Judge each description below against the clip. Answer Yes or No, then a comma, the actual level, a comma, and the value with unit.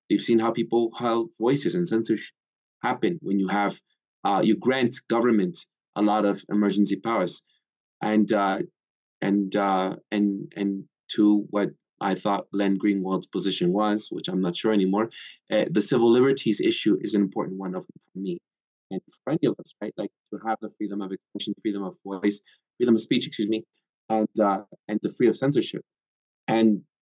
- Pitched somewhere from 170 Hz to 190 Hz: No, low, 105 Hz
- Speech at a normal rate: Yes, average, 180 wpm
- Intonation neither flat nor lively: No, narrow, 2.3 semitones